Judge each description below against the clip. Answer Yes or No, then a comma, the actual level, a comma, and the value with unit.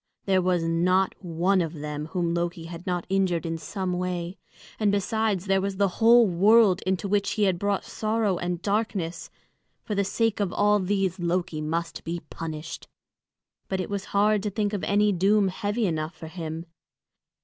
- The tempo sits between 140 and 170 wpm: No, average, 180 wpm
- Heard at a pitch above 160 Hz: Yes, medium, 185 Hz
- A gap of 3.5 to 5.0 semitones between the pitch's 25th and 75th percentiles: No, average, 3.0 semitones